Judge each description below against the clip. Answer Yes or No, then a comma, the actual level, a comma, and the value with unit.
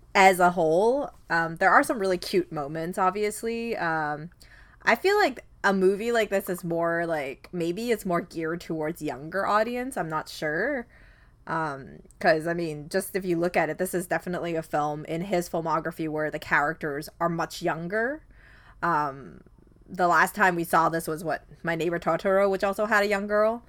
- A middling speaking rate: Yes, average, 185 wpm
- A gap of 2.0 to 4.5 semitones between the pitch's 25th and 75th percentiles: Yes, average, 3.2 semitones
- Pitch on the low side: No, medium, 175 Hz